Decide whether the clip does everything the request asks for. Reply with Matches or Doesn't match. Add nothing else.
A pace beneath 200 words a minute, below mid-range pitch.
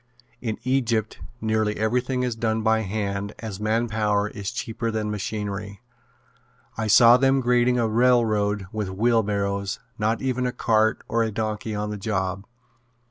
Matches